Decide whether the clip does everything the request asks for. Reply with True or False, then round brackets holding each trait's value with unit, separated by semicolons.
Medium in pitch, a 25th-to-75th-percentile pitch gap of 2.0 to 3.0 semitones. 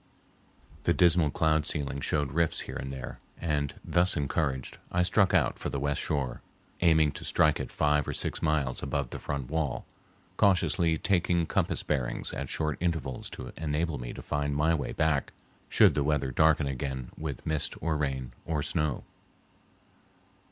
False (75 Hz; 2.6 semitones)